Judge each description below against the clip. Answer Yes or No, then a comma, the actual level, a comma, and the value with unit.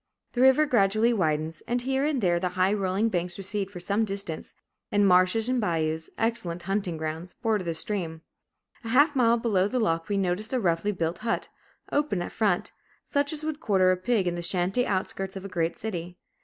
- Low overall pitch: No, high, 195 Hz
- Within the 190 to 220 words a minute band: Yes, average, 200 wpm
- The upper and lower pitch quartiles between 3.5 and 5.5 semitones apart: Yes, average, 4.5 semitones